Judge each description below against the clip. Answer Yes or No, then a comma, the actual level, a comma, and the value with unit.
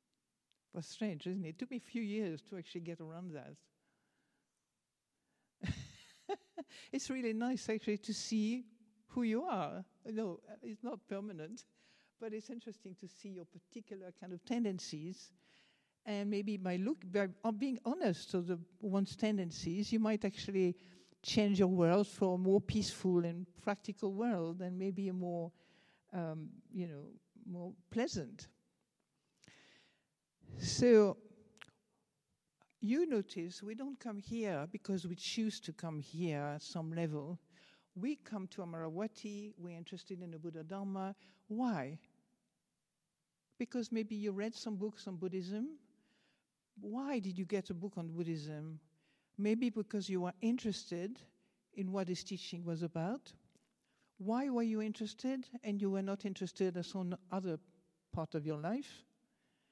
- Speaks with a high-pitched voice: Yes, high, 195 Hz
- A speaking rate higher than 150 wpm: No, average, 145 wpm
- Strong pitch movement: No, average, 3.9 semitones